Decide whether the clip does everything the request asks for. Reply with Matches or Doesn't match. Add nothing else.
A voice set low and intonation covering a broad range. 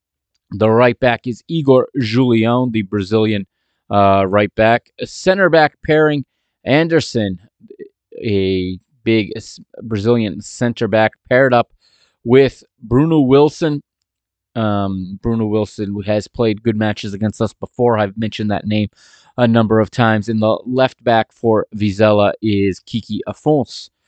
Doesn't match